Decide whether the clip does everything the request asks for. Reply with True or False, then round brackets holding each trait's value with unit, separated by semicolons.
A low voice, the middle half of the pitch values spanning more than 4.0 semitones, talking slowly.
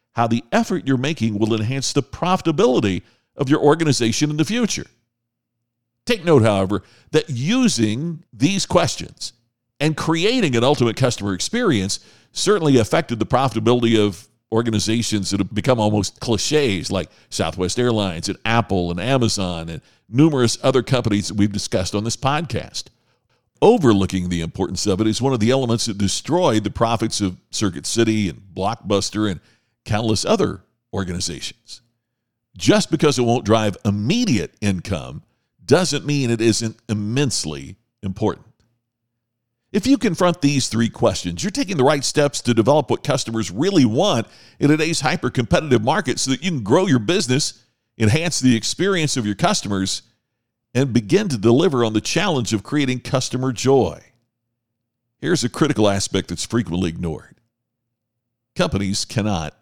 False (115 Hz; 4.6 semitones; 150 wpm)